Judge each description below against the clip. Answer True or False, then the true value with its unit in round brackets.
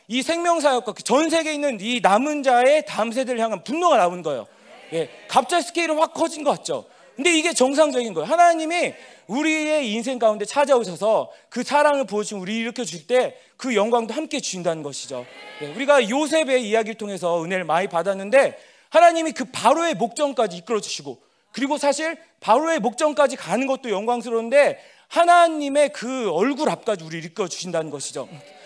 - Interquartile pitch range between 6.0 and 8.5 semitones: True (6.4 semitones)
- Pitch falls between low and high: False (255 Hz)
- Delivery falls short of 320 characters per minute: False (395 characters per minute)